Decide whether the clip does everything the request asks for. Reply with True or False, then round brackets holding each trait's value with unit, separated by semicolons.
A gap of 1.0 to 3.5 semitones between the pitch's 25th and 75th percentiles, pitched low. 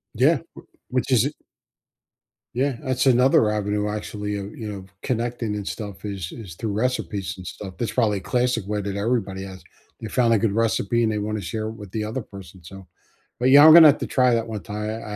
True (2.9 semitones; 105 Hz)